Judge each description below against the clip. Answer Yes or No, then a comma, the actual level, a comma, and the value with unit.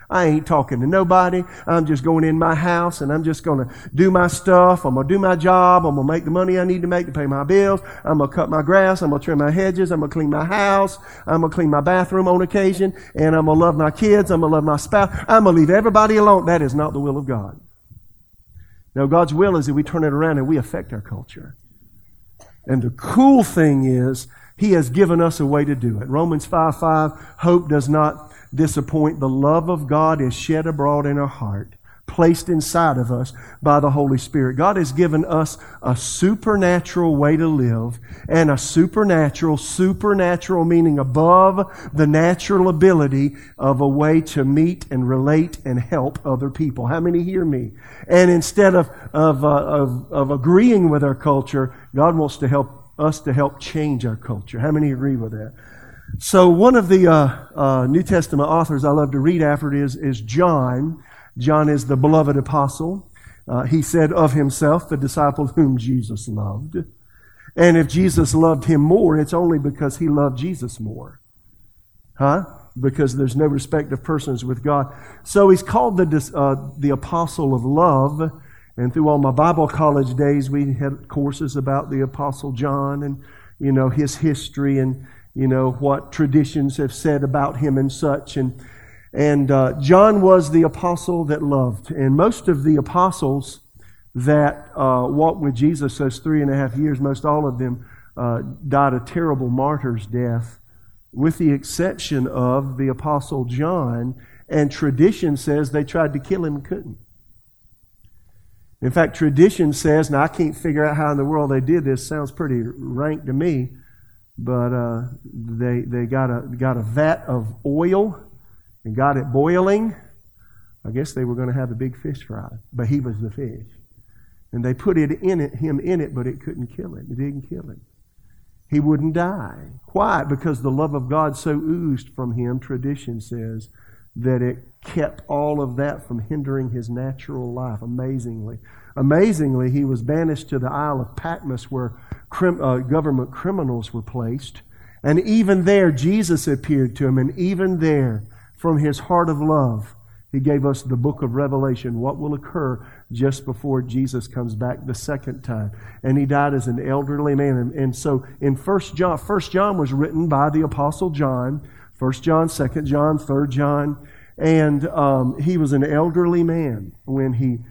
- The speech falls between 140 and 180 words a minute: No, average, 190 wpm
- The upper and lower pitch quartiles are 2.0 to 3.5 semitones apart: No, average, 3.9 semitones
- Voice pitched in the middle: Yes, medium, 145 Hz